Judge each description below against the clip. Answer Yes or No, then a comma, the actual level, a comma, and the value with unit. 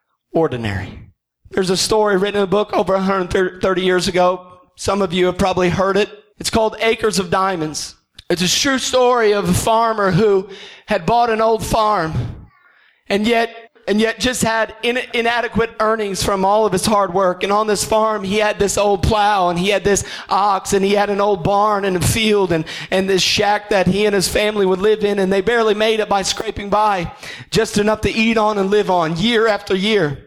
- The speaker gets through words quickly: Yes, fast, 210 wpm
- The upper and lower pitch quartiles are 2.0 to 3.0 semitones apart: Yes, narrow, 2.4 semitones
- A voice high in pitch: Yes, high, 200 Hz